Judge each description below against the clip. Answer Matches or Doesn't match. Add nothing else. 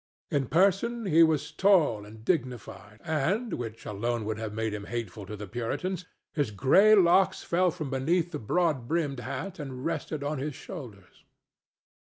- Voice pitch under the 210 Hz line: Matches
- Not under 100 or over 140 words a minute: Doesn't match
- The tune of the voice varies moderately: Doesn't match